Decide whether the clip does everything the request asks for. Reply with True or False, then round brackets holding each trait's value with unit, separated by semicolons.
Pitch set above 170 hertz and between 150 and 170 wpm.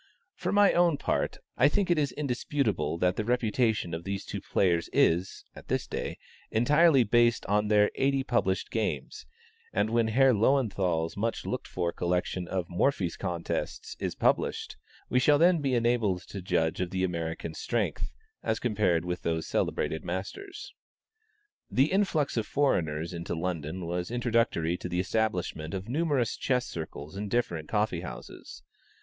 False (105 Hz; 155 wpm)